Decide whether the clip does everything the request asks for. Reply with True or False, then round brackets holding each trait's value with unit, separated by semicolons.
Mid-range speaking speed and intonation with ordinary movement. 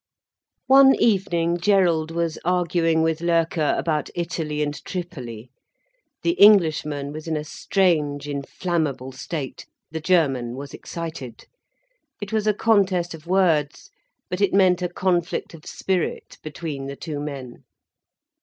False (130 wpm; 3.5 semitones)